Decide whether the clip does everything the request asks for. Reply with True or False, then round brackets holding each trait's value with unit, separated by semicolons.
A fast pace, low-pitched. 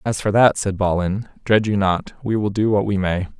True (250 wpm; 100 Hz)